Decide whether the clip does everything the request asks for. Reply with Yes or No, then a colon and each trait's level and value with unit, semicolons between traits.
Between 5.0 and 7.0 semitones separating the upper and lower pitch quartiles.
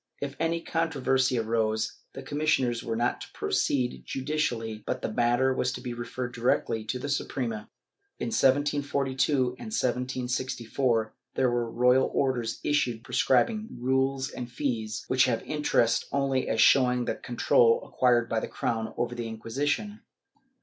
No: average, 2.7 semitones